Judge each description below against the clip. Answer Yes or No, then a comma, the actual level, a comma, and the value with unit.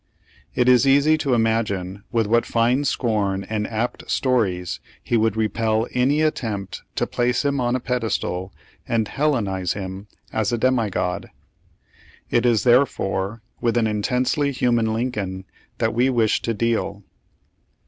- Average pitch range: Yes, average, 3.2 semitones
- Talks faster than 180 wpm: No, average, 140 wpm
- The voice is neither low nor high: No, low, 115 Hz